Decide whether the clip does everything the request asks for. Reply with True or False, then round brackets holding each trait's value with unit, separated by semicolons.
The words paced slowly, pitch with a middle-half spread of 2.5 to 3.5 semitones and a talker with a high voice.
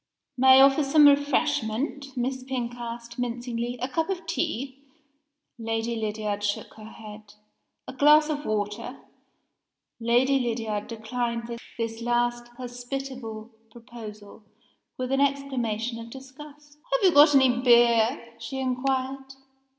True (125 wpm; 2.9 semitones; 245 Hz)